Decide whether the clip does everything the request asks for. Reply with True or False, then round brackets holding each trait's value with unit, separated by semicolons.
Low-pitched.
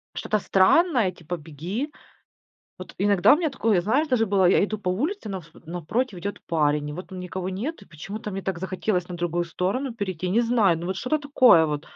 False (190 Hz)